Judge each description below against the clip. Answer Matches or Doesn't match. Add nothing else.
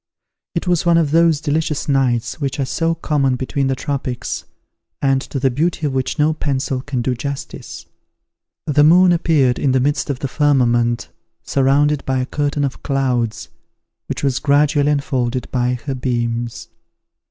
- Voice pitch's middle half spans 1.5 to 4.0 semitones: Matches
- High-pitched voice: Doesn't match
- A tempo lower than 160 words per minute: Doesn't match